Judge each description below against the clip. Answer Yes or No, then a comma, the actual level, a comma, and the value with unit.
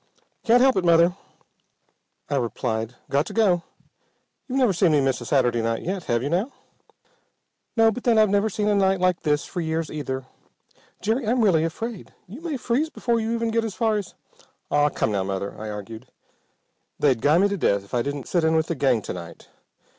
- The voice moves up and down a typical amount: No, wide, 8.8 semitones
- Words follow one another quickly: Yes, fast, 210 wpm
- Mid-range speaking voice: Yes, medium, 170 Hz